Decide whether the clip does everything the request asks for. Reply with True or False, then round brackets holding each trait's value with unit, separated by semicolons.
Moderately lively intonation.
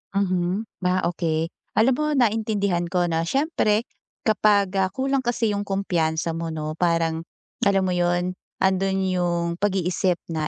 True (3.2 semitones)